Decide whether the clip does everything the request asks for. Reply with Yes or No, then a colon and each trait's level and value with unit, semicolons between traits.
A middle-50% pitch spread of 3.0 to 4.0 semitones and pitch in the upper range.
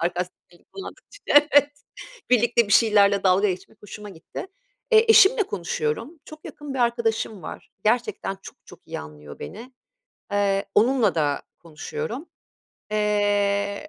No: average, 5.0 semitones; high, 210 Hz